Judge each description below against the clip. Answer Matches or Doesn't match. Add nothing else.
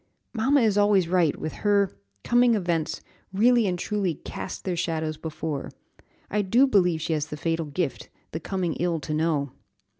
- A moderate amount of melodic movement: Matches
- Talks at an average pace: Matches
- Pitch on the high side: Doesn't match